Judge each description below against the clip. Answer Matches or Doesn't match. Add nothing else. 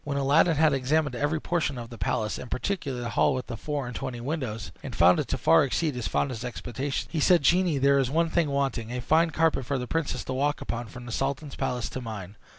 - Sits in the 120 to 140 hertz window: Matches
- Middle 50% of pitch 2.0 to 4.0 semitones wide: Matches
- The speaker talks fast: Matches